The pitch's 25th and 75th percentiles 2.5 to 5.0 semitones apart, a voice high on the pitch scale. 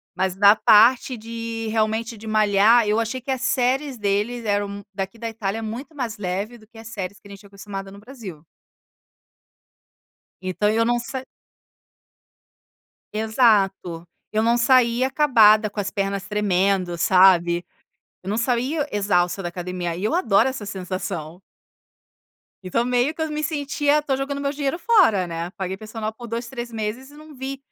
Yes: average, 4.1 semitones; high, 220 Hz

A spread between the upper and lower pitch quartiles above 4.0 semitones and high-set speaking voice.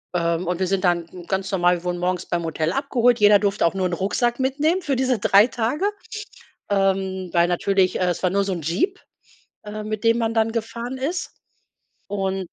Yes: average, 4.5 semitones; high, 195 Hz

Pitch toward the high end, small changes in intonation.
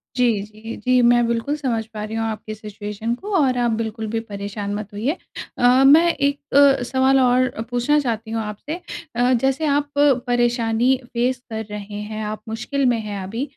No: high, 240 Hz; average, 3.4 semitones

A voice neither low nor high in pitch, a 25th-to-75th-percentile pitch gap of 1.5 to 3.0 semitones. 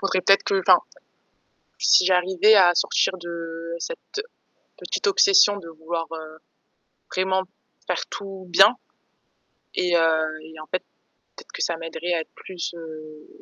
Yes: medium, 175 Hz; narrow, 2.6 semitones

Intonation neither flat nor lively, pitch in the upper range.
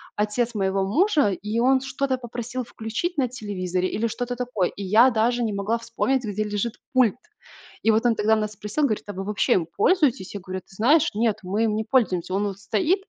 Yes: average, 3.5 semitones; high, 220 Hz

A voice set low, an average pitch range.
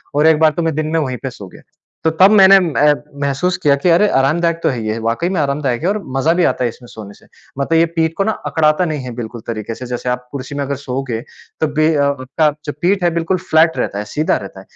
No: medium, 150 Hz; average, 4.6 semitones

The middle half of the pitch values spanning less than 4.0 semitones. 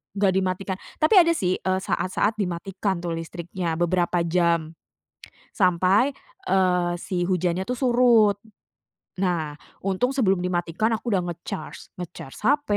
Yes: average, 2.8 semitones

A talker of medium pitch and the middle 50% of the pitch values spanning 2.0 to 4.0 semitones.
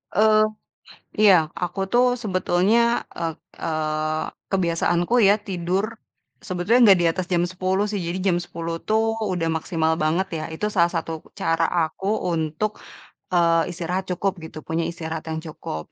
Yes: medium, 175 Hz; average, 3.3 semitones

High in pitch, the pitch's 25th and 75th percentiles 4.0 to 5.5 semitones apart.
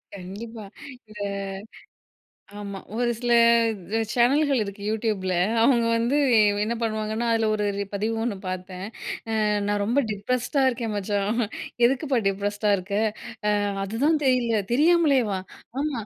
No: high, 225 Hz; average, 3.2 semitones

